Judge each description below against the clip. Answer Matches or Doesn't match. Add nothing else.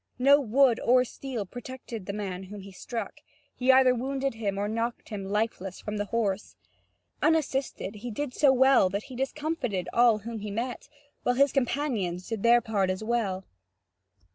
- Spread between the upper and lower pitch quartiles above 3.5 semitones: Matches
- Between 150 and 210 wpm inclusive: Matches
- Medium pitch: Doesn't match